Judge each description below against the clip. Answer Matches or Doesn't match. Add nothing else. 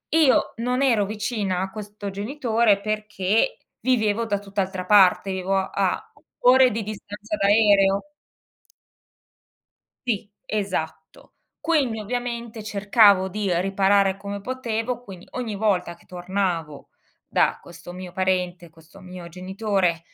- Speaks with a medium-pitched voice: Doesn't match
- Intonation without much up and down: Doesn't match